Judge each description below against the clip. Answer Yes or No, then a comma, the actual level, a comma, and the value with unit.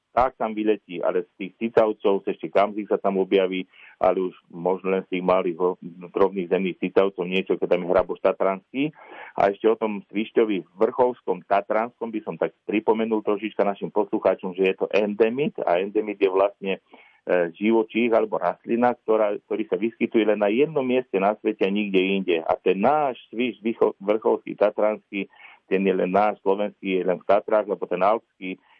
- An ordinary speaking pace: No, fast, 180 wpm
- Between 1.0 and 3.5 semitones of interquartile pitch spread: Yes, narrow, 2.6 semitones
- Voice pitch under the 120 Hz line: Yes, low, 105 Hz